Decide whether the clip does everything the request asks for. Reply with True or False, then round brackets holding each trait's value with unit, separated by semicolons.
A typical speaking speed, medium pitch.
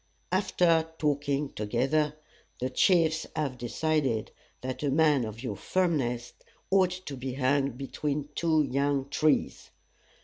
False (125 wpm; 145 Hz)